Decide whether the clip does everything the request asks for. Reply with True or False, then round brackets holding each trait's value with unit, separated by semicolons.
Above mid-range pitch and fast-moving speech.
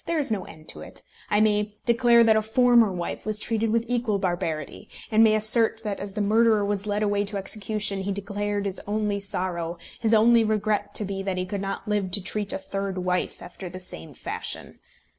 True (205 Hz; 215 wpm)